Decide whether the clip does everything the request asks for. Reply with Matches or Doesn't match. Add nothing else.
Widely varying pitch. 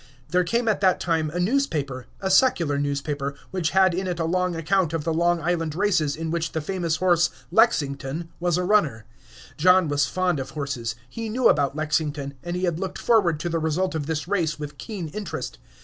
Doesn't match